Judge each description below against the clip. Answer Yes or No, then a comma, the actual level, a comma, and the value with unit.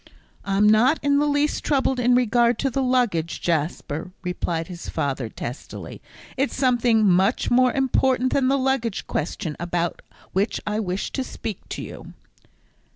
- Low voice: No, high, 230 Hz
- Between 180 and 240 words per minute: No, average, 155 wpm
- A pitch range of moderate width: No, wide, 6.5 semitones